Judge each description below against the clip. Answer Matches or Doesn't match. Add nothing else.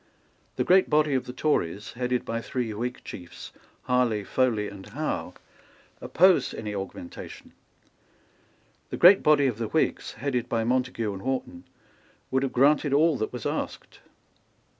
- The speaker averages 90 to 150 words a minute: Matches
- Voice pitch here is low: Matches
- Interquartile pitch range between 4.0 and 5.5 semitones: Matches